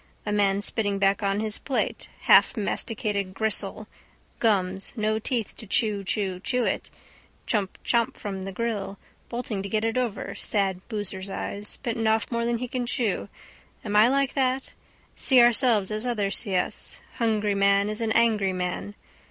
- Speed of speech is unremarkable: Yes, average, 160 wpm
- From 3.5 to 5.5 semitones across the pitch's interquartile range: No, average, 2.8 semitones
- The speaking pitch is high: Yes, high, 215 Hz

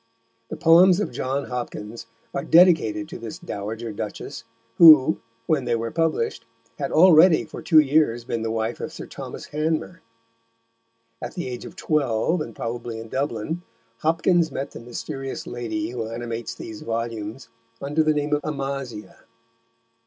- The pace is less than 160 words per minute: Yes, average, 150 wpm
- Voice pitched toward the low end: Yes, low, 130 Hz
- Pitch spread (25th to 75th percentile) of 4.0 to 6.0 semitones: Yes, wide, 5.4 semitones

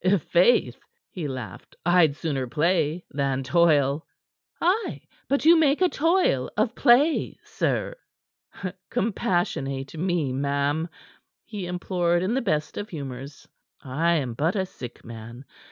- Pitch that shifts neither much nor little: No, wide, 6.6 semitones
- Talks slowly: Yes, slow, 125 wpm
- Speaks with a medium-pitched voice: Yes, medium, 170 Hz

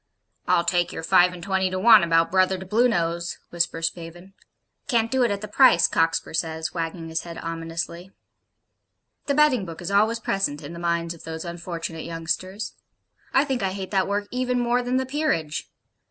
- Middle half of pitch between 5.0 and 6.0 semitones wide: No, average, 4.3 semitones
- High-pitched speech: No, medium, 180 Hz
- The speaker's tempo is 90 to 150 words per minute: No, average, 185 wpm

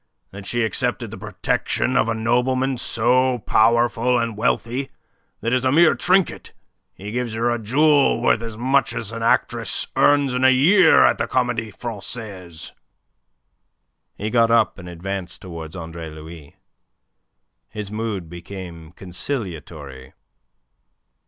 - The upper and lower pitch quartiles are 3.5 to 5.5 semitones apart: Yes, average, 5.1 semitones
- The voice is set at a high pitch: No, low, 115 Hz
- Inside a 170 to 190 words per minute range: No, slow, 135 wpm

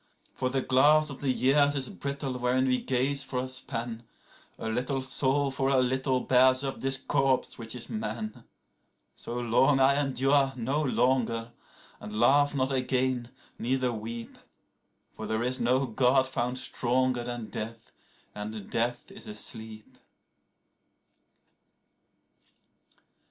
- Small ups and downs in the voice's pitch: Yes, narrow, 2.2 semitones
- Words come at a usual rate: No, slow, 130 wpm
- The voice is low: Yes, low, 130 Hz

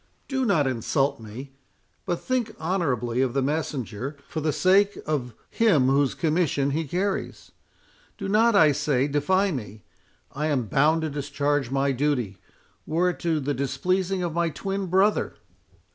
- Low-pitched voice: No, medium, 150 Hz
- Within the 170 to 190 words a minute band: No, average, 145 wpm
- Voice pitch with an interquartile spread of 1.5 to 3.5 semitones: No, average, 5.2 semitones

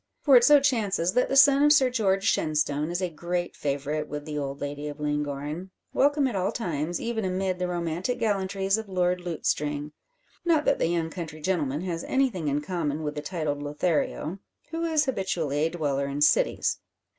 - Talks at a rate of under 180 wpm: No, average, 190 wpm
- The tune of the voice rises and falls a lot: Yes, wide, 5.8 semitones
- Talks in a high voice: No, medium, 175 Hz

